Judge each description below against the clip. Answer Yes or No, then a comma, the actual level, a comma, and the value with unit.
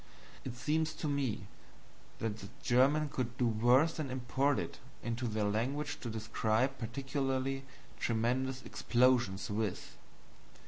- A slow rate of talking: Yes, slow, 125 wpm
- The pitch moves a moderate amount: Yes, average, 3.2 semitones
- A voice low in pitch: Yes, low, 125 Hz